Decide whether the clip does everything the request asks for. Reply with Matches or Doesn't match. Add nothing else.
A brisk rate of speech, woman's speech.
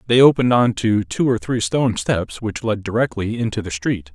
Doesn't match